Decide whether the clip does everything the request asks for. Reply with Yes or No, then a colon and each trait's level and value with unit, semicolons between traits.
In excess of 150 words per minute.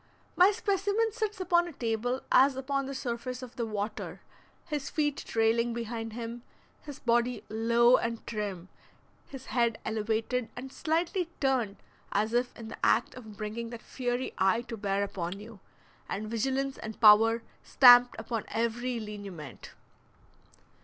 No: average, 145 wpm